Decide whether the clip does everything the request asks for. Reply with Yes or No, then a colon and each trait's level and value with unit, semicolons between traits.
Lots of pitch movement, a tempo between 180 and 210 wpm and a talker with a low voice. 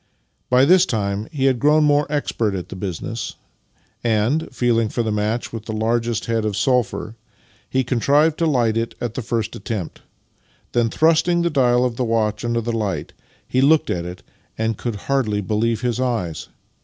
No: average, 3.4 semitones; average, 190 wpm; low, 115 Hz